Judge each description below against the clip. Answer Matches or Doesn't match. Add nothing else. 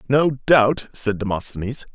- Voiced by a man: Matches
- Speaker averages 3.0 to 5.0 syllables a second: Matches